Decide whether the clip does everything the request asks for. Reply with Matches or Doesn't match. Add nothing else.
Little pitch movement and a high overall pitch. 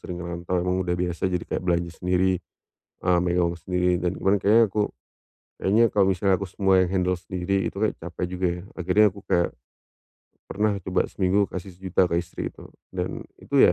Doesn't match